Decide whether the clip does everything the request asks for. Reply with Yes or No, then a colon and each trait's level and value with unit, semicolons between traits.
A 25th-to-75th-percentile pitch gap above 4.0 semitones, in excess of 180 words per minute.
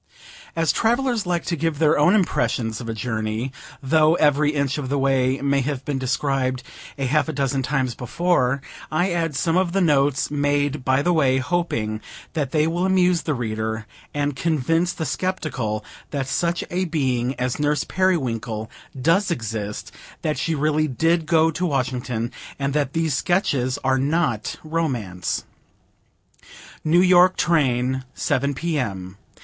No: average, 4.5 semitones; average, 155 wpm